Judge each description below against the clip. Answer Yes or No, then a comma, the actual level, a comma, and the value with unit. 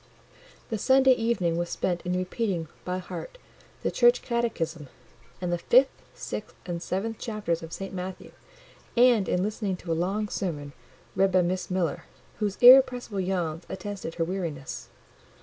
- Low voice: No, medium, 185 Hz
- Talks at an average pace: Yes, average, 150 wpm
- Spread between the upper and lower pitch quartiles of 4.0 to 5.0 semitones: Yes, average, 4.3 semitones